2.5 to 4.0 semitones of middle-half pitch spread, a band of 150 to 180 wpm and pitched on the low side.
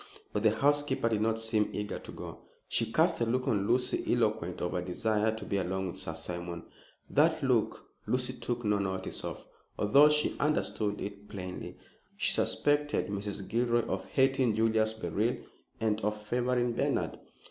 Yes: average, 3.4 semitones; average, 170 wpm; low, 110 Hz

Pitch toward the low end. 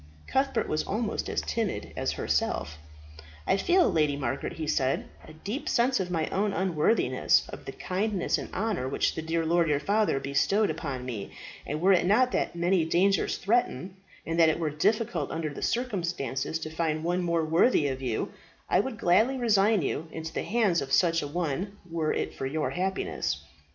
No: medium, 170 Hz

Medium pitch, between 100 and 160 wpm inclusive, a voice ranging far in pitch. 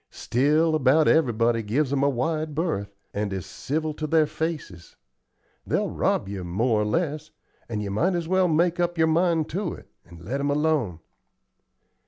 No: medium, 150 Hz; average, 175 wpm; wide, 6.5 semitones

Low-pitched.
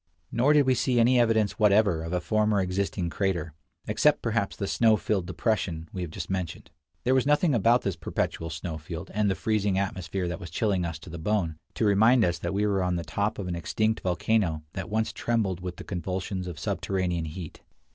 Yes: very low, 95 Hz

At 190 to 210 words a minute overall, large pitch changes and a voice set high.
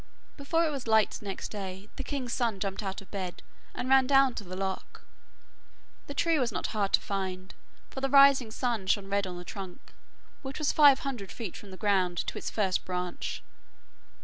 Yes: average, 200 wpm; wide, 5.9 semitones; high, 210 Hz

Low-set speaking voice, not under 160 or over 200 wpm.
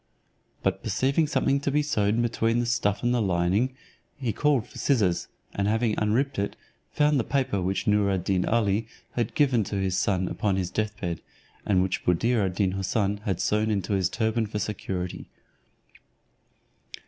Yes: low, 105 Hz; average, 170 wpm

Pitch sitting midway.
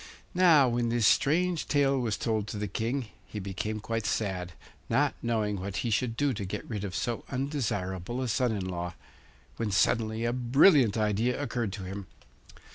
No: low, 115 Hz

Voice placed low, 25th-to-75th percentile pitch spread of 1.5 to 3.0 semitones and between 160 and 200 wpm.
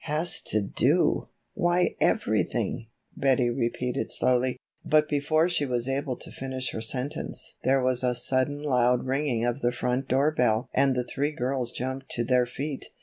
Yes: low, 130 Hz; narrow, 2.6 semitones; average, 165 wpm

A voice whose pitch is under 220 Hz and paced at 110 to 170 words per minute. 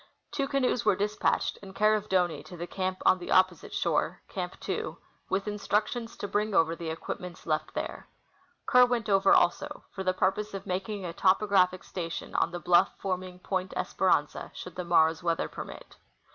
No: high, 190 Hz; average, 185 wpm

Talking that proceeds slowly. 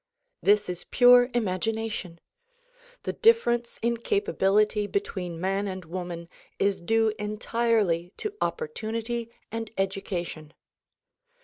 Yes: slow, 100 wpm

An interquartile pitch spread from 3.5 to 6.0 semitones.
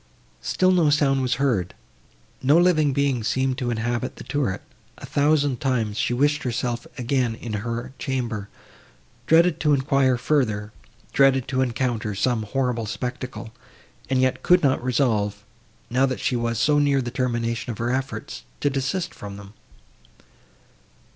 No: average, 3.0 semitones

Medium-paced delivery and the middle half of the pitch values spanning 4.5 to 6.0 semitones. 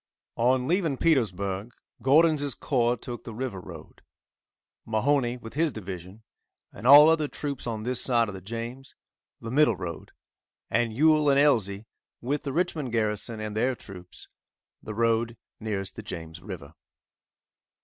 Yes: average, 145 wpm; average, 4.8 semitones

